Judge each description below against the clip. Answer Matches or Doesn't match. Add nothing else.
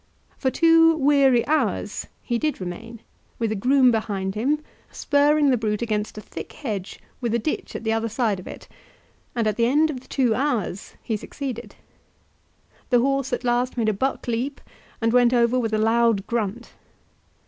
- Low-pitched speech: Doesn't match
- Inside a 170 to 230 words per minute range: Matches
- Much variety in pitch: Doesn't match